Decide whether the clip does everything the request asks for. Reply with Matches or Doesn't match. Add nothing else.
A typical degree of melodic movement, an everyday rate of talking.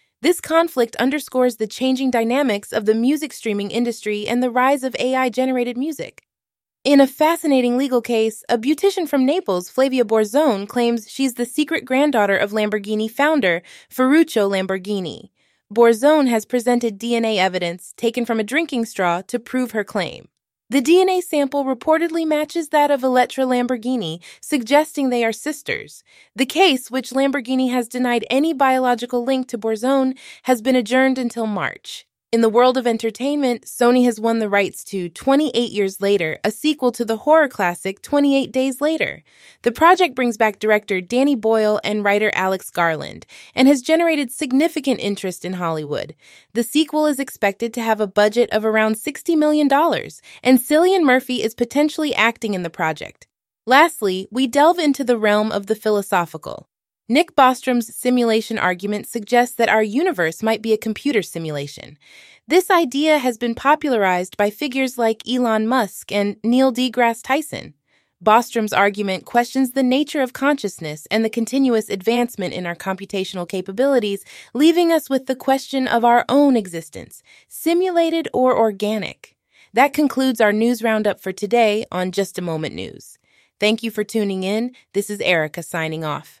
Matches